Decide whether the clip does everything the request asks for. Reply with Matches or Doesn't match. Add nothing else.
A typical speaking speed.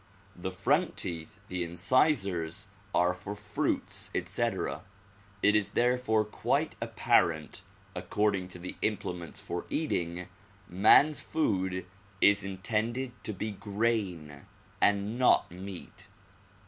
Doesn't match